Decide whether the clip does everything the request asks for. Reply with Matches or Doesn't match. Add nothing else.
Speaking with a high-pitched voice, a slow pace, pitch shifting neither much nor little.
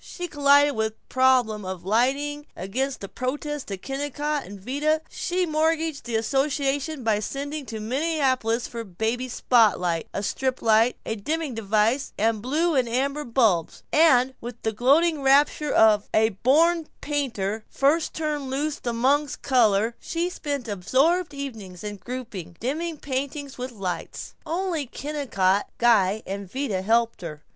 Doesn't match